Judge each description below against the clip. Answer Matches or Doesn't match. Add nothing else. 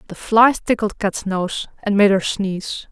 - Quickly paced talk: Doesn't match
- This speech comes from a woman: Matches